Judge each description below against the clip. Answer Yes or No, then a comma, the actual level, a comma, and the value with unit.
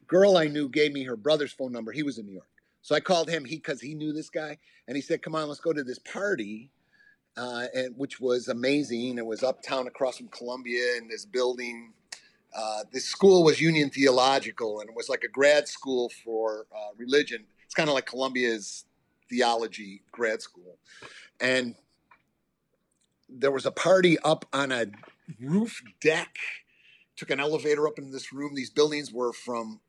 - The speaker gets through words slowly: No, average, 185 wpm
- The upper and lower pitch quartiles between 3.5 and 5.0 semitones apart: Yes, average, 4.0 semitones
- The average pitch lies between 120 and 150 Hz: Yes, low, 135 Hz